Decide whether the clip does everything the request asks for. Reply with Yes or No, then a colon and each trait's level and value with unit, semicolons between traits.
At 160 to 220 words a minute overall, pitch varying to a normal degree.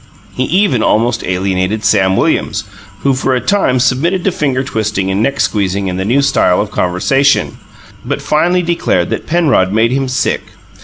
No: average, 170 wpm; wide, 6.3 semitones